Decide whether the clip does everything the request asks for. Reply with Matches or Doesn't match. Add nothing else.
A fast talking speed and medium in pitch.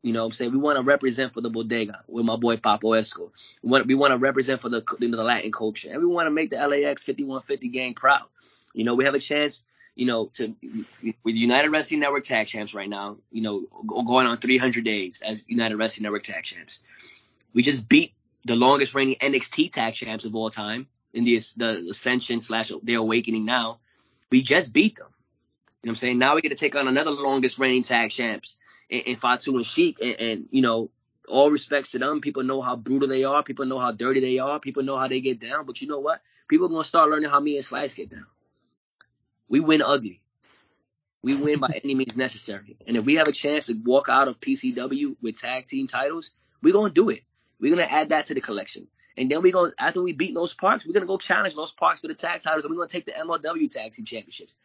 Doesn't match